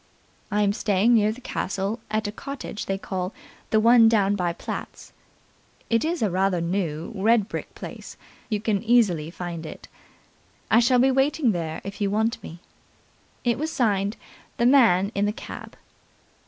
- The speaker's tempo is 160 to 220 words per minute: Yes, average, 170 wpm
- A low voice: No, high, 210 Hz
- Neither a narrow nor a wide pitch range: Yes, average, 3.6 semitones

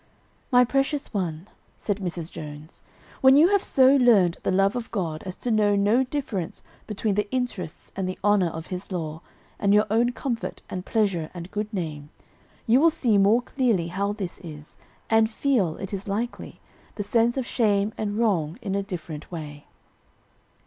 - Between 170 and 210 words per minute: Yes, average, 175 wpm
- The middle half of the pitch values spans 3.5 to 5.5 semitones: Yes, average, 5.0 semitones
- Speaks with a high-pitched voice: Yes, high, 205 Hz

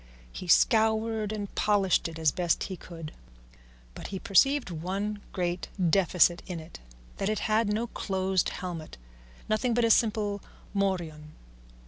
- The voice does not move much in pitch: No, average, 3.7 semitones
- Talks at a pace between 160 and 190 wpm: No, average, 140 wpm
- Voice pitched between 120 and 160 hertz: No, high, 195 Hz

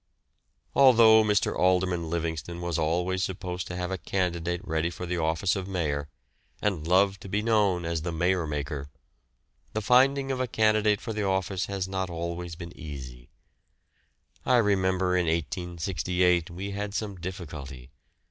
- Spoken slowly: No, average, 155 wpm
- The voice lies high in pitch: No, very low, 90 Hz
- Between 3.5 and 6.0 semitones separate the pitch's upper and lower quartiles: No, average, 2.9 semitones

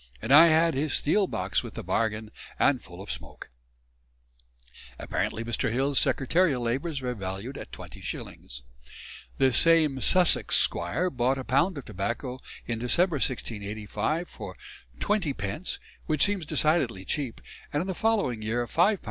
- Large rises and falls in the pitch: Yes, wide, 6.6 semitones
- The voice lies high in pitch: No, low, 135 Hz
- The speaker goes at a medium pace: Yes, average, 150 wpm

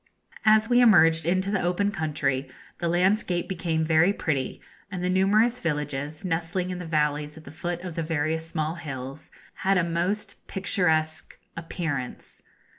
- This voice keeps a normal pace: Yes, average, 155 wpm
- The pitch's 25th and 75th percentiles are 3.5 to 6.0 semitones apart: No, average, 3.1 semitones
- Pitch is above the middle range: No, medium, 165 Hz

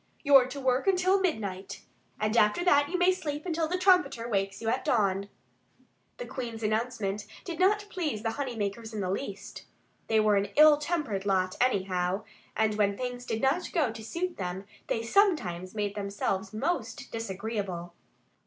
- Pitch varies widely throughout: Yes, wide, 7.0 semitones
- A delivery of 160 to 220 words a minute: Yes, average, 170 wpm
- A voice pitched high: Yes, high, 225 Hz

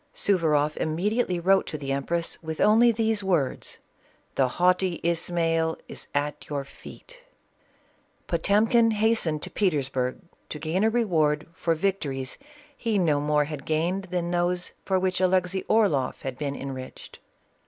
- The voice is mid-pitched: Yes, medium, 170 Hz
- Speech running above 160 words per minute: No, average, 145 wpm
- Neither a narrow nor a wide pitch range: Yes, average, 4.6 semitones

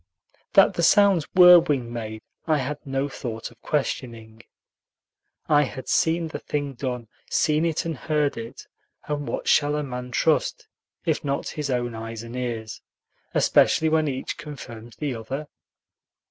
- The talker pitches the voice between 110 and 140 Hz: Yes, low, 135 Hz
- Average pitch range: Yes, average, 4.1 semitones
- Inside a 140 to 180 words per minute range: Yes, average, 155 wpm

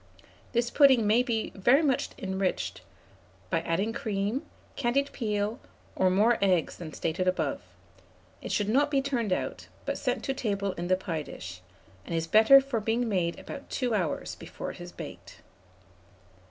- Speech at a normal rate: Yes, average, 165 wpm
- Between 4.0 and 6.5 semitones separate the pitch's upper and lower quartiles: Yes, average, 5.1 semitones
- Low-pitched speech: No, high, 215 Hz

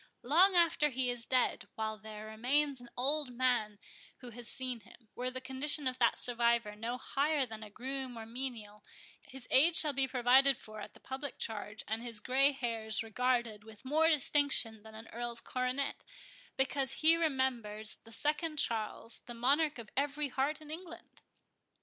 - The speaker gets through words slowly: No, average, 175 wpm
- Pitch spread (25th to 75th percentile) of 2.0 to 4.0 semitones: Yes, average, 3.6 semitones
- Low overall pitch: No, very high, 250 Hz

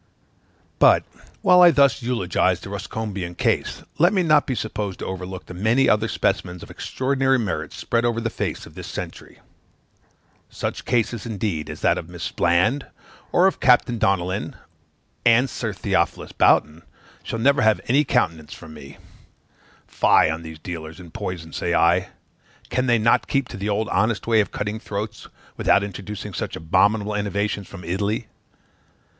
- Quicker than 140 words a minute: Yes, average, 160 wpm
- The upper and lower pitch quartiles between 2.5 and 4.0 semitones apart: No, average, 4.7 semitones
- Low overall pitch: Yes, low, 105 Hz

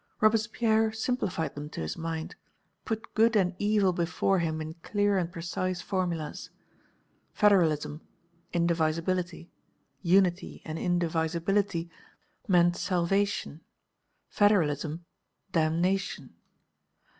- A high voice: No, medium, 175 Hz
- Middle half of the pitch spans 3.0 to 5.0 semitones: Yes, average, 3.4 semitones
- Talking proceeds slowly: Yes, slow, 90 wpm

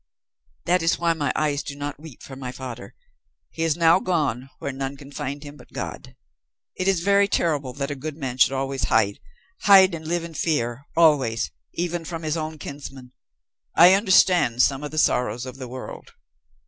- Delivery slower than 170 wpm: No, average, 190 wpm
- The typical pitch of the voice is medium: Yes, medium, 145 Hz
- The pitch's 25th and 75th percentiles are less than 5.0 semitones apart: Yes, average, 3.9 semitones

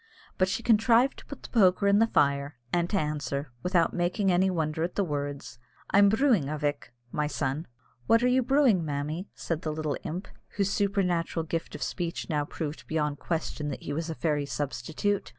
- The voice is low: No, medium, 165 Hz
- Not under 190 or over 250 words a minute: Yes, average, 200 wpm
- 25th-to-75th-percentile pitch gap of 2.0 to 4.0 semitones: No, average, 5.1 semitones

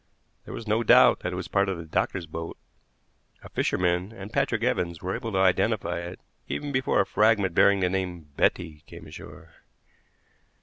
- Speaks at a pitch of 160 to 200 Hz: No, very low, 95 Hz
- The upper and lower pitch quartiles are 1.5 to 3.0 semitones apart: Yes, narrow, 2.6 semitones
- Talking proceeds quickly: No, average, 180 wpm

